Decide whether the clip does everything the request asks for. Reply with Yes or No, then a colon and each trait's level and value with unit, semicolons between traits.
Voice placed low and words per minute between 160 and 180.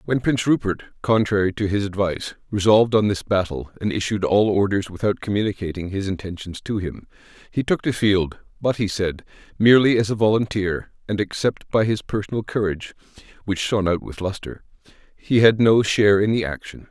Yes: low, 100 Hz; average, 175 wpm